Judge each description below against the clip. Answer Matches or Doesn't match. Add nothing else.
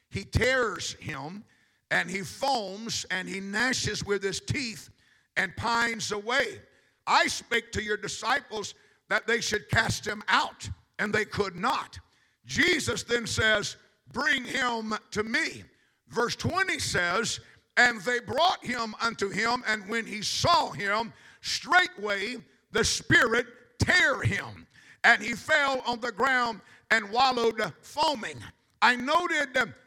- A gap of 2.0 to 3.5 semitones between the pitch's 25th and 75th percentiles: Matches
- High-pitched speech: Matches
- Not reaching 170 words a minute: Matches